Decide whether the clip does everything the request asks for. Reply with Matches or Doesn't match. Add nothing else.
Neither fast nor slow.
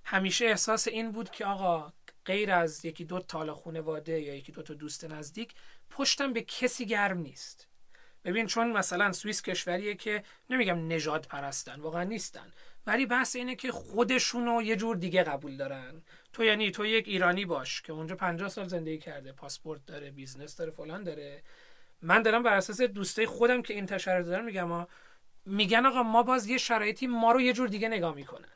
Doesn't match